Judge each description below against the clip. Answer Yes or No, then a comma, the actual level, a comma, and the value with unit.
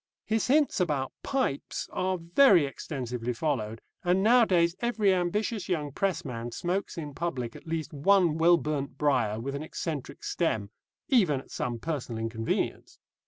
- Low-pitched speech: No, medium, 160 Hz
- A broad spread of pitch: Yes, wide, 5.9 semitones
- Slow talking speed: No, average, 145 wpm